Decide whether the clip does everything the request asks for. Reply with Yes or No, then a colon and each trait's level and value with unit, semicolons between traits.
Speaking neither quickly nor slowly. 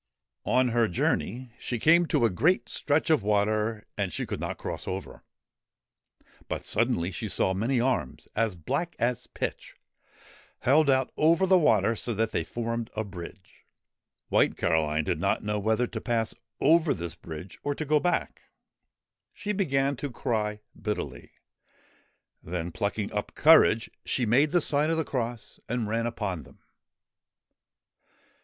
Yes: average, 155 wpm